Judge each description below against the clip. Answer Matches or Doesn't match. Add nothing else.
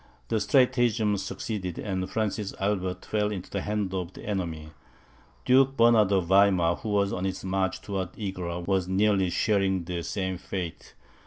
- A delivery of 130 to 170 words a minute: Matches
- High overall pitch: Doesn't match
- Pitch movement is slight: Matches